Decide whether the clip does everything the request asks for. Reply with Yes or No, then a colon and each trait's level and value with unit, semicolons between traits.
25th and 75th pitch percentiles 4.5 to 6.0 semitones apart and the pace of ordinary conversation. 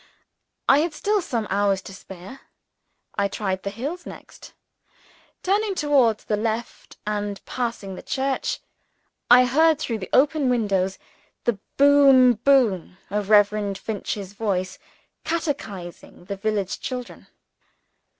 No: wide, 5.5 semitones; slow, 120 wpm